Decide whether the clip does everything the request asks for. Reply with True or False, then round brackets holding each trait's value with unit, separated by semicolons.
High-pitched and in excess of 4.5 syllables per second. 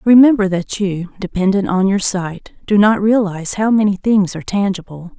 True (195 Hz; 5.1 syllables/s)